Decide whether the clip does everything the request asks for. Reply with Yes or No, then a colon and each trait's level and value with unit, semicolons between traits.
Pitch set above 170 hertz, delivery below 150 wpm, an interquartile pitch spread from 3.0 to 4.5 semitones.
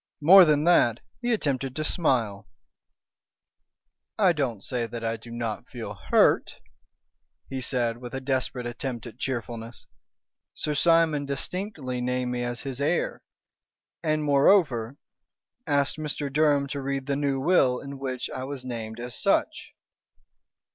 No: low, 135 Hz; average, 140 wpm; average, 3.5 semitones